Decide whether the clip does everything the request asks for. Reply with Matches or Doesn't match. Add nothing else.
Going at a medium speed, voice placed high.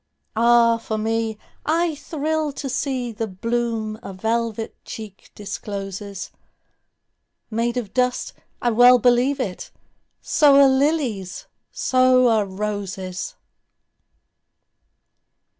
Doesn't match